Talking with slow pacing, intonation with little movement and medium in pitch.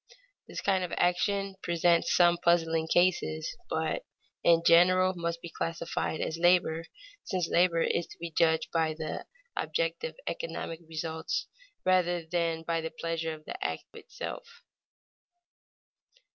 Yes: slow, 130 wpm; narrow, 1.7 semitones; medium, 170 Hz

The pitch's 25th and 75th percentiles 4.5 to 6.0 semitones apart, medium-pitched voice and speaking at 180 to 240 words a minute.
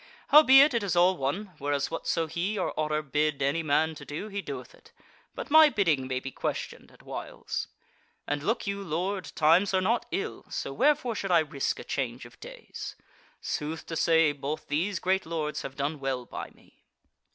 Yes: average, 5.3 semitones; medium, 165 Hz; average, 190 wpm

